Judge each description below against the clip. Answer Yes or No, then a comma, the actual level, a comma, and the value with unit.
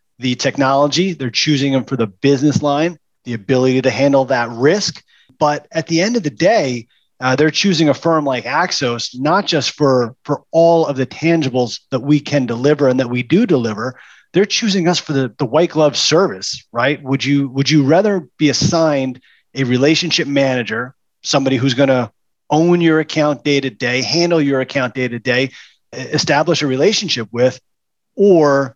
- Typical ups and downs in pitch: Yes, average, 3.4 semitones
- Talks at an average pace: Yes, average, 180 wpm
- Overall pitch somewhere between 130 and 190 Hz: Yes, medium, 140 Hz